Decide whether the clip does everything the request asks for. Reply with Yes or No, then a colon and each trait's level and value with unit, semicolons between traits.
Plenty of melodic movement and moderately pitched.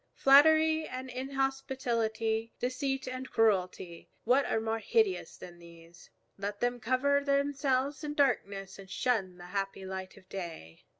No: wide, 5.7 semitones; high, 245 Hz